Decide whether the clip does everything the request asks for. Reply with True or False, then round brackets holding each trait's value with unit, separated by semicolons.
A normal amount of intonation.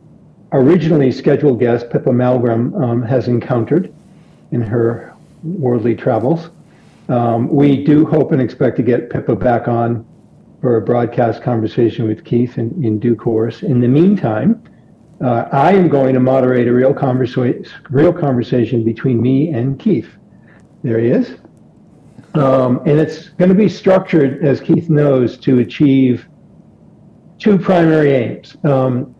True (4.3 semitones)